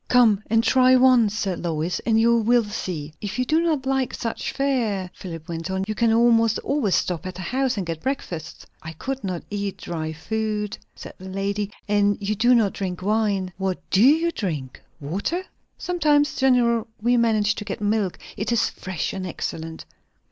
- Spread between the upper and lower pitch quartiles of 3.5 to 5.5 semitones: Yes, average, 4.4 semitones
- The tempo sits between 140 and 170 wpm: No, average, 185 wpm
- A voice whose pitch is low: No, high, 210 Hz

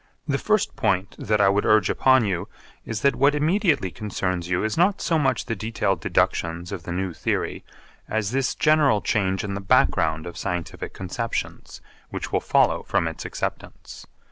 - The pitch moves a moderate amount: No, wide, 6.5 semitones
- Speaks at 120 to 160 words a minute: No, average, 175 wpm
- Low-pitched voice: Yes, low, 105 Hz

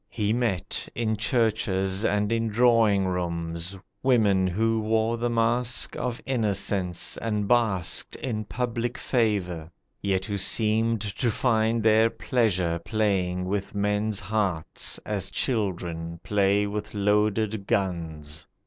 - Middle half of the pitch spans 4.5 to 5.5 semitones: No, average, 3.1 semitones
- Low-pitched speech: Yes, low, 105 Hz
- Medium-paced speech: No, slow, 120 wpm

